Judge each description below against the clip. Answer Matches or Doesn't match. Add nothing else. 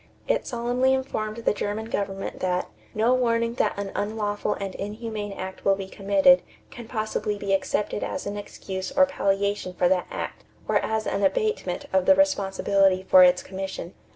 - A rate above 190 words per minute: Doesn't match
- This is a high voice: Matches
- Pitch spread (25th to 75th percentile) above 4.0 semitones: Doesn't match